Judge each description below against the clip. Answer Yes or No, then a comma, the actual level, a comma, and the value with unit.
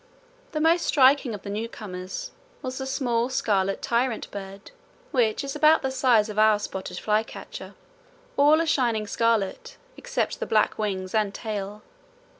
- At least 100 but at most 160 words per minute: Yes, average, 150 wpm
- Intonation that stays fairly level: No, average, 4.2 semitones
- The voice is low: No, high, 225 Hz